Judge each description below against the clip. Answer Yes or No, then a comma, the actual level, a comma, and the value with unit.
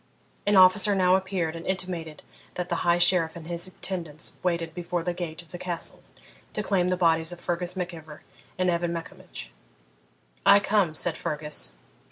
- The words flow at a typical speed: Yes, average, 175 wpm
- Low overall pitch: No, medium, 175 Hz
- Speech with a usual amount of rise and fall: No, narrow, 1.8 semitones